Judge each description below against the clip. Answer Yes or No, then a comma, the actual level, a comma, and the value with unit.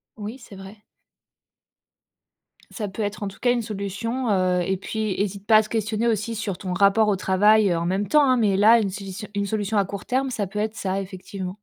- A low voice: No, high, 205 Hz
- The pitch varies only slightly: Yes, narrow, 2.3 semitones